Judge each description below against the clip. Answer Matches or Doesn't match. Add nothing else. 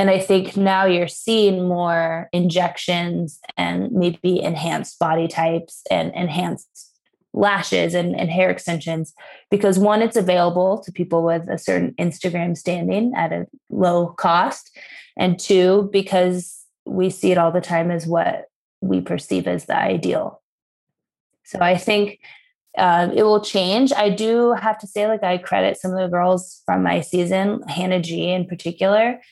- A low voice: Doesn't match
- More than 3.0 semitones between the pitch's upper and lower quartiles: Doesn't match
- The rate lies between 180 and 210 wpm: Doesn't match